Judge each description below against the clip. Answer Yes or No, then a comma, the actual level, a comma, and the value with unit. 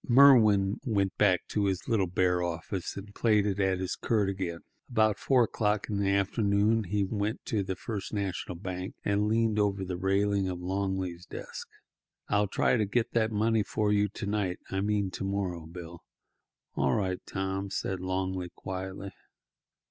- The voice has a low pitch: Yes, low, 100 Hz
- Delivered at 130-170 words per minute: Yes, average, 165 wpm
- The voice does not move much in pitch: Yes, narrow, 2.1 semitones